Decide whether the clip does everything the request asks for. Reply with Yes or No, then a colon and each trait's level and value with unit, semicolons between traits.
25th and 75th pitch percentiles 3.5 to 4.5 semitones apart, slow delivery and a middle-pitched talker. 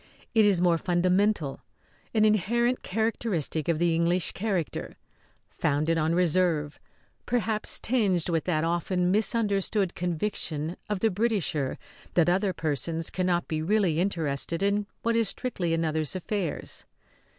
Yes: average, 4.1 semitones; slow, 130 wpm; medium, 180 Hz